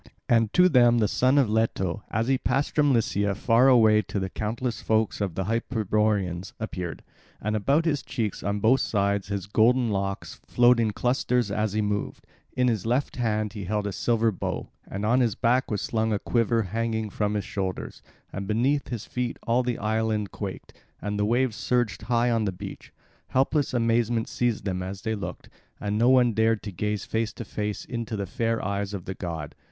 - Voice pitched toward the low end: Yes, low, 110 Hz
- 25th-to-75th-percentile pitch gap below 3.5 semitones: Yes, average, 2.8 semitones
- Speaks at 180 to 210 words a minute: Yes, average, 200 wpm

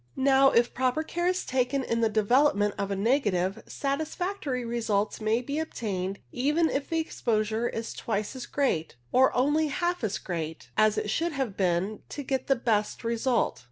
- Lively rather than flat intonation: No, average, 4.8 semitones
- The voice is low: No, high, 240 Hz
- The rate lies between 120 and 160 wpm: No, average, 175 wpm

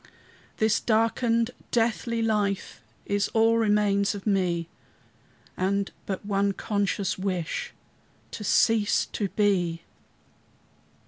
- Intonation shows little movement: Yes, narrow, 2.3 semitones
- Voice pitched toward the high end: Yes, high, 205 Hz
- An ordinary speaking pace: No, slow, 100 wpm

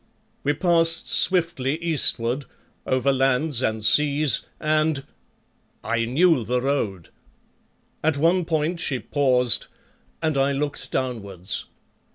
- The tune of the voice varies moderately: Yes, average, 4.1 semitones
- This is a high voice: No, medium, 140 Hz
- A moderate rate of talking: No, slow, 110 wpm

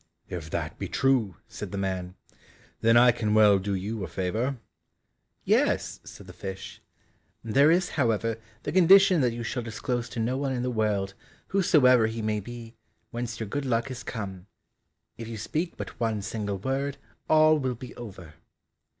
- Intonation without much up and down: No, average, 4.1 semitones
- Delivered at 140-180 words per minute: Yes, average, 175 wpm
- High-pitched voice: No, low, 115 Hz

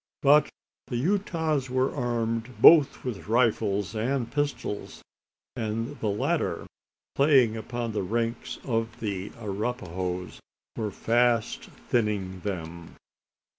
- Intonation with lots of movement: No, average, 3.5 semitones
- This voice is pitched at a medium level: No, low, 115 Hz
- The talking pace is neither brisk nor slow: No, slow, 105 wpm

